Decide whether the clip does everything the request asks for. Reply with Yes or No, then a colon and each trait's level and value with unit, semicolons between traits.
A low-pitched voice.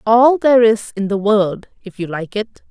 No: high, 215 Hz